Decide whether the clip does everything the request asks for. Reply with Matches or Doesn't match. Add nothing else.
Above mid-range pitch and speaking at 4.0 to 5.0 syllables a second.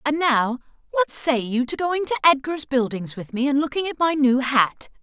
Matches